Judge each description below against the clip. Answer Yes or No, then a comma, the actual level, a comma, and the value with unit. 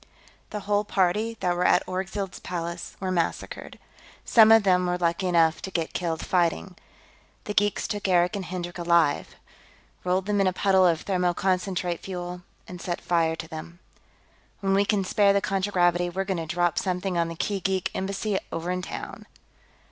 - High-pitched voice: No, medium, 180 Hz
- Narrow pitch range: Yes, narrow, 2.0 semitones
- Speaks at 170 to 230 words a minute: Yes, average, 180 wpm